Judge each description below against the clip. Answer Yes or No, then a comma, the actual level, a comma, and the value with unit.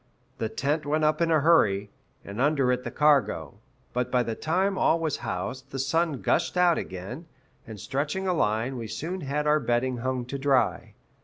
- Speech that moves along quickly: No, average, 190 wpm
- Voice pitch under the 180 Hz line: Yes, low, 135 Hz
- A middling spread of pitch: Yes, average, 4.6 semitones